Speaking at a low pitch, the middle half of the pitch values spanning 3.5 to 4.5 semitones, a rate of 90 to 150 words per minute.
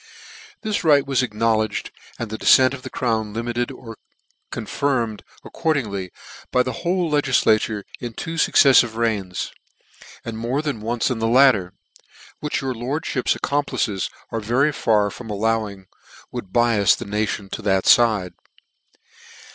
Yes: low, 115 Hz; average, 3.8 semitones; average, 145 wpm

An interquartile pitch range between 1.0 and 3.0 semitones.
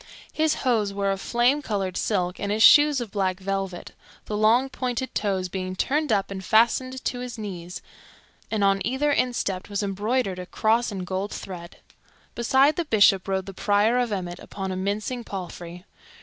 No: average, 4.2 semitones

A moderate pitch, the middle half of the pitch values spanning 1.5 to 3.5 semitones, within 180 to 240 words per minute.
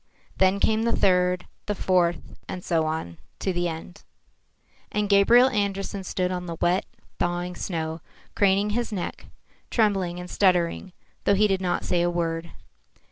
No: medium, 180 Hz; narrow, 2.4 semitones; average, 155 wpm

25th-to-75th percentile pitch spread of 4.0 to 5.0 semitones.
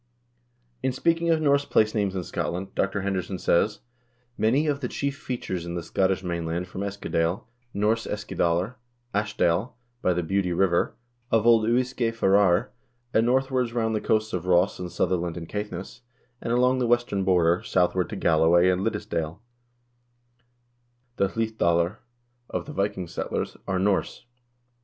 Yes: average, 4.5 semitones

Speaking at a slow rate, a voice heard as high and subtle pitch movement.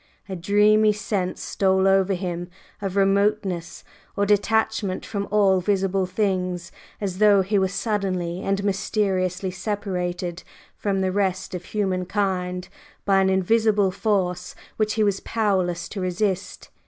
Yes: slow, 130 wpm; high, 195 Hz; narrow, 1.9 semitones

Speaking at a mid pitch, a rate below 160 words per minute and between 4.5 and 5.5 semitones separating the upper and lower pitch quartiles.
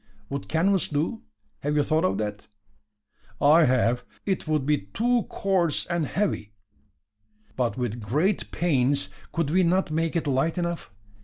Yes: medium, 155 Hz; average, 150 wpm; average, 5.1 semitones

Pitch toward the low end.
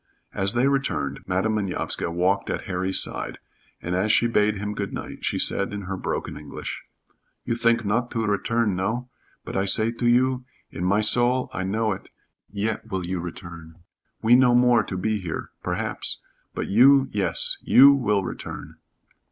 Yes: low, 105 Hz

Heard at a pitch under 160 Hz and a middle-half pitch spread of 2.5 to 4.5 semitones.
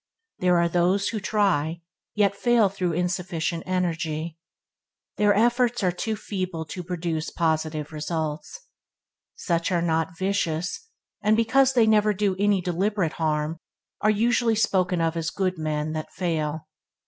No: medium, 180 Hz; average, 4.1 semitones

